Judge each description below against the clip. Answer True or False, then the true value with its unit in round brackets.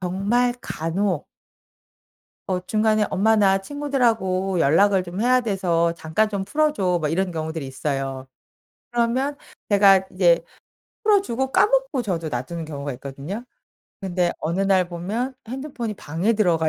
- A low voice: False (190 Hz)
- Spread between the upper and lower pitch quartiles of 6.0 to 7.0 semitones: False (5.5 semitones)